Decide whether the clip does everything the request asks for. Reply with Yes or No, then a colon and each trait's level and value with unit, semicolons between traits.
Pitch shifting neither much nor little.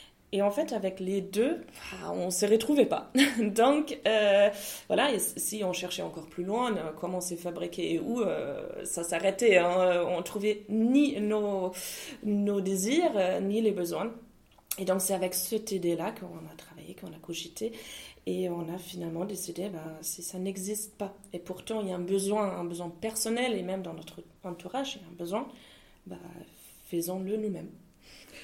Yes: average, 3.6 semitones